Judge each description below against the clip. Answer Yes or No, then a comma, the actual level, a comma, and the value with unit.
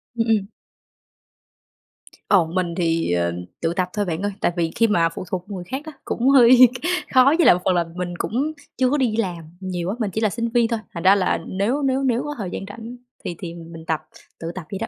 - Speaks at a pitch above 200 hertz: No, high, 195 Hz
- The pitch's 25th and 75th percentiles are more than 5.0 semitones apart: Yes, wide, 5.5 semitones